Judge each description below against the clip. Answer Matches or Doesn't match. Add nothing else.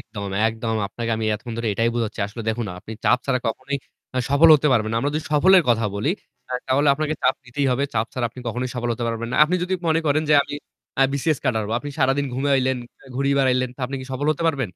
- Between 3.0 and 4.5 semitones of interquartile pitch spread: Matches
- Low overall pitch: Matches